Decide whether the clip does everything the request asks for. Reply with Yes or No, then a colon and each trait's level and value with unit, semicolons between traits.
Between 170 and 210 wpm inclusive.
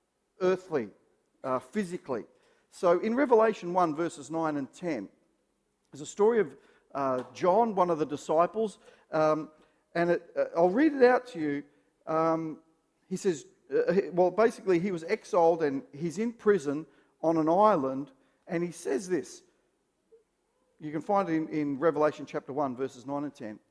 No: average, 160 wpm